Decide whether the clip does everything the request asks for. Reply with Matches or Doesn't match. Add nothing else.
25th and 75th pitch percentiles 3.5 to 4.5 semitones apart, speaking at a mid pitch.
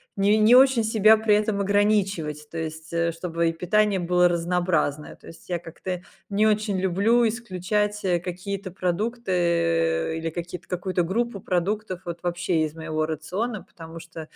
Matches